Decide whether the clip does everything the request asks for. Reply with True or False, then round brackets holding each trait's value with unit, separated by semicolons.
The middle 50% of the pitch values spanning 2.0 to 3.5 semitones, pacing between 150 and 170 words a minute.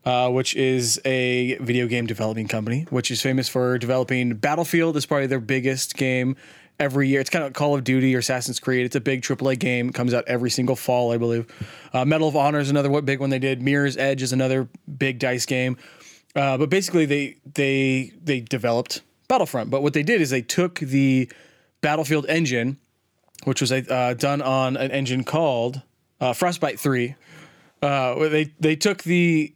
False (2.7 semitones; 195 wpm)